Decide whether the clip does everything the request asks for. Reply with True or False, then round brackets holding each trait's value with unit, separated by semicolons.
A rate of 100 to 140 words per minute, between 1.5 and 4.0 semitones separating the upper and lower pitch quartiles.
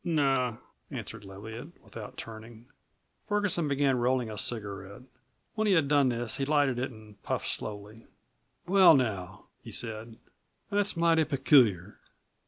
False (135 wpm; 5.2 semitones)